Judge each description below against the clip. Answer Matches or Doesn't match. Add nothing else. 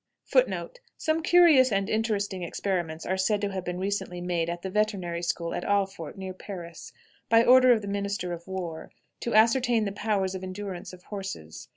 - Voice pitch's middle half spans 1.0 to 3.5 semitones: Matches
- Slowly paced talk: Doesn't match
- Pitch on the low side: Doesn't match